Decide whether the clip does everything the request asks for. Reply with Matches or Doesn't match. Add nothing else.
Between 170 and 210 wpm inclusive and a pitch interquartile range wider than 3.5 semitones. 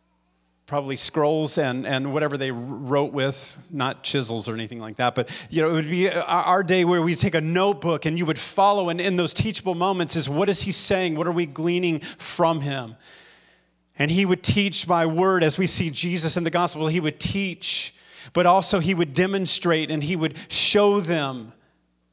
Matches